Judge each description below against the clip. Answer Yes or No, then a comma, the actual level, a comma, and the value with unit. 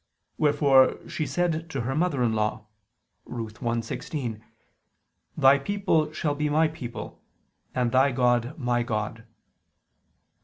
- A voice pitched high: No, low, 130 Hz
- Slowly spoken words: Yes, slow, 120 wpm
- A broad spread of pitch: No, average, 4.4 semitones